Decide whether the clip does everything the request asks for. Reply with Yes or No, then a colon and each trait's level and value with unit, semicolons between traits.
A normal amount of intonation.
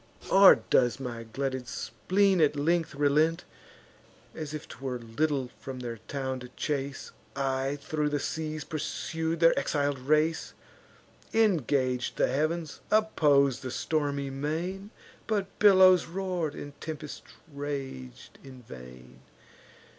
Yes: average, 3.6 semitones